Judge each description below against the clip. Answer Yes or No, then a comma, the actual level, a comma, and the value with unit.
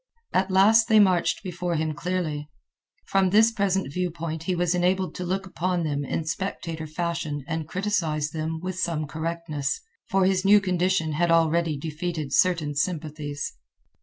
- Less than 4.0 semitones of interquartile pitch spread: Yes, average, 3.1 semitones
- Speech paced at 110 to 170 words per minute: Yes, average, 160 wpm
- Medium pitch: Yes, medium, 170 Hz